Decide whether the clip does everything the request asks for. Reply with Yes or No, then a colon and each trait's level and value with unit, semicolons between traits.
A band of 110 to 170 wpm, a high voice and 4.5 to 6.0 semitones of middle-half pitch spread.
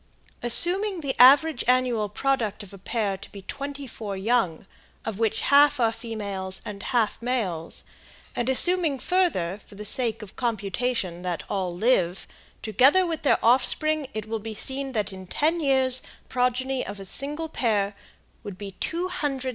Yes: average, 165 wpm; high, 240 Hz; average, 5.3 semitones